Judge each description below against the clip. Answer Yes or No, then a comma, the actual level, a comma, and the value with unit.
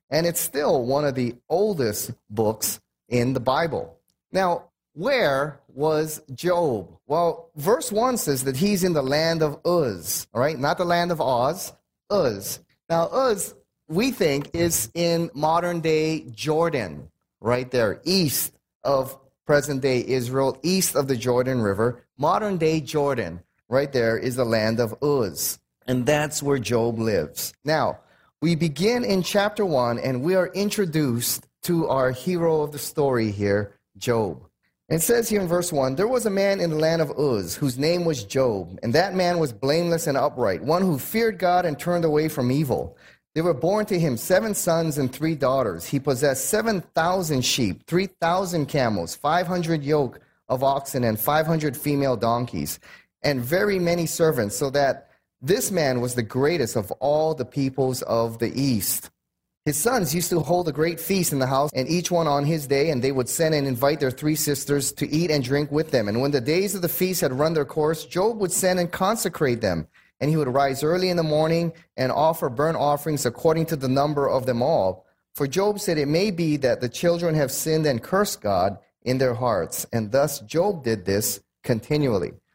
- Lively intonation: No, average, 4.5 semitones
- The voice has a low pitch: No, medium, 150 Hz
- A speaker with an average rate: Yes, average, 190 wpm